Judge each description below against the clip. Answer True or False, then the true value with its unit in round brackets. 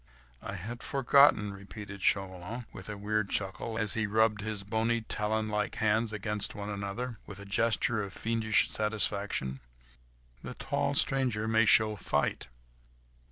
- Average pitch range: False (1.9 semitones)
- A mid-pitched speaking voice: False (105 Hz)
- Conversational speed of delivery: True (150 wpm)